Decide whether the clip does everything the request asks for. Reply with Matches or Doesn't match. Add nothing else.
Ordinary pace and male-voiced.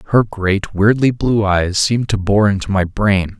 Matches